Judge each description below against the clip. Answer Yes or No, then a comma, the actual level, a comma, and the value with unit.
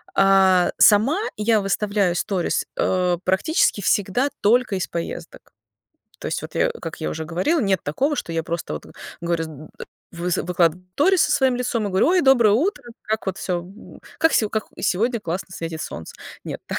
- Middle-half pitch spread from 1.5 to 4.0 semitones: No, average, 5.2 semitones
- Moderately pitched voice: No, high, 195 Hz